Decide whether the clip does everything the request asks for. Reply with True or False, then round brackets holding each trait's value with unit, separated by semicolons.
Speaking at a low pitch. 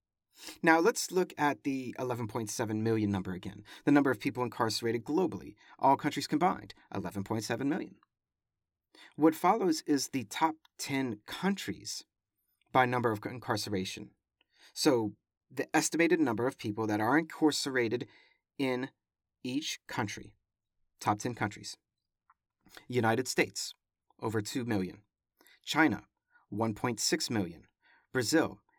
True (120 Hz)